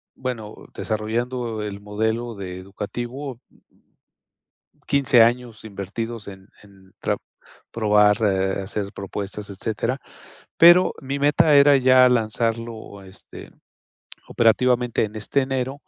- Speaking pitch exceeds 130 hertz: No, low, 115 Hz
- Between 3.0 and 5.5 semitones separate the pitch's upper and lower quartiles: Yes, average, 3.6 semitones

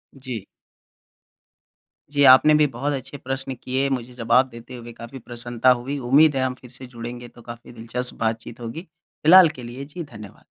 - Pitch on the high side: No, low, 125 Hz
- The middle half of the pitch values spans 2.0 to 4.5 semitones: Yes, narrow, 2.4 semitones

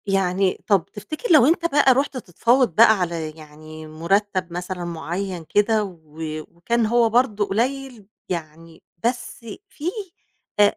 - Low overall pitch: No, high, 195 Hz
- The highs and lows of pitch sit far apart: Yes, wide, 6.0 semitones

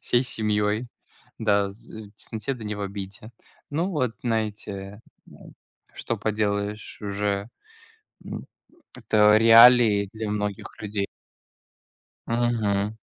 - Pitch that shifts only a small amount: Yes, narrow, 1.9 semitones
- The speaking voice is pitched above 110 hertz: No, low, 105 Hz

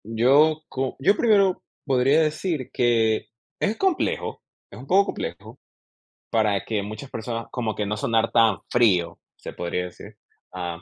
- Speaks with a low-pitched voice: Yes, low, 120 Hz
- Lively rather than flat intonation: Yes, wide, 6.1 semitones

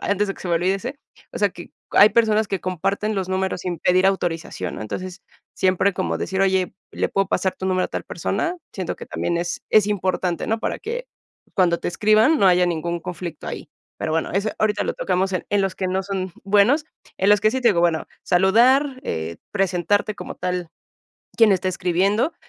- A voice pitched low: No, high, 190 Hz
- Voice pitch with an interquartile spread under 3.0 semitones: Yes, narrow, 2.6 semitones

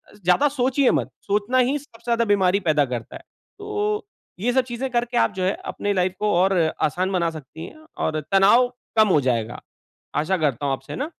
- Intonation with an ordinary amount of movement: No, wide, 7.1 semitones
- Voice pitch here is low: No, high, 200 Hz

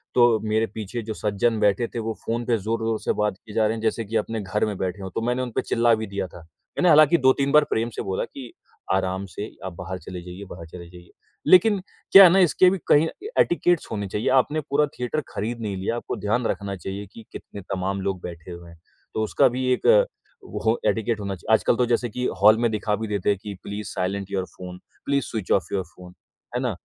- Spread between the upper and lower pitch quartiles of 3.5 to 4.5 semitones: Yes, average, 3.8 semitones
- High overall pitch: No, low, 110 Hz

